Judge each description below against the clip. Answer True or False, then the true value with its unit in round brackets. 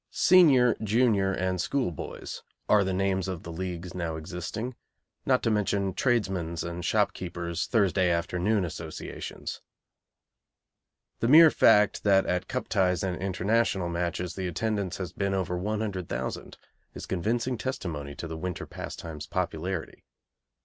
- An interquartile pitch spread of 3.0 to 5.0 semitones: True (3.5 semitones)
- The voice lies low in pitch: True (95 Hz)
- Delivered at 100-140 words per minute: True (135 wpm)